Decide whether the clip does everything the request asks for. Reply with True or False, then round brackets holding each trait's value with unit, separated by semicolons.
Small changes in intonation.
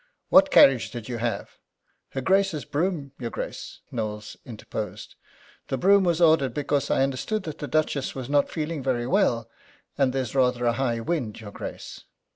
False (4.7 semitones)